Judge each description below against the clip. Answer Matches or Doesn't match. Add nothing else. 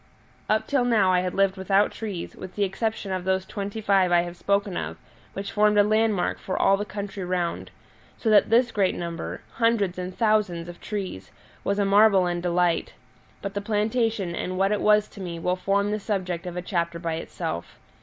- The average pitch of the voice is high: Matches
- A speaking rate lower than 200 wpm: Doesn't match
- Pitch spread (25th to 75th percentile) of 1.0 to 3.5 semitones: Matches